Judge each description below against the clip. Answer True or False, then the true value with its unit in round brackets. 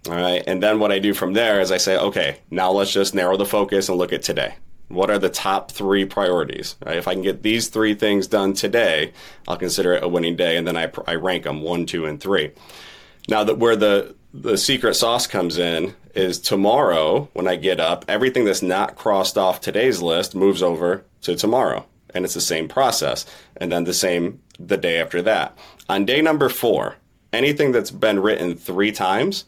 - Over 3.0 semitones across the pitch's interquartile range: False (2.5 semitones)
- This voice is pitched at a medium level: False (95 Hz)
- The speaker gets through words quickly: True (215 wpm)